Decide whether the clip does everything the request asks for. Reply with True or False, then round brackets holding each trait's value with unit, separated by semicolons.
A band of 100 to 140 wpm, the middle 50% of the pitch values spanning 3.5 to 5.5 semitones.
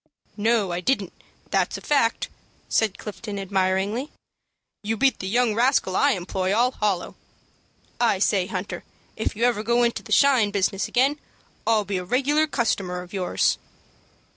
False (155 wpm; 4.1 semitones)